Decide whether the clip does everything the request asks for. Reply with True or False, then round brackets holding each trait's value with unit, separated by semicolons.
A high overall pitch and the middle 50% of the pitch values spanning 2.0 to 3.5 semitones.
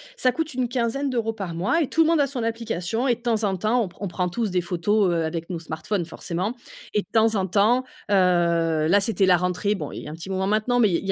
False (205 Hz; 4.8 semitones)